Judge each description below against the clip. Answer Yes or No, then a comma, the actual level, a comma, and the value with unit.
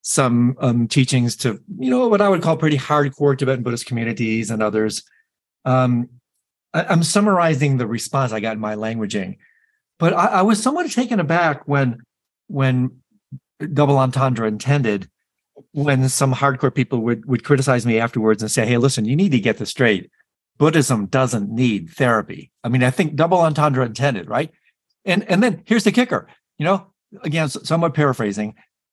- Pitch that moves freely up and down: Yes, wide, 5.9 semitones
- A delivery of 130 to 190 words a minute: Yes, average, 170 wpm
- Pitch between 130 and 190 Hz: Yes, low, 135 Hz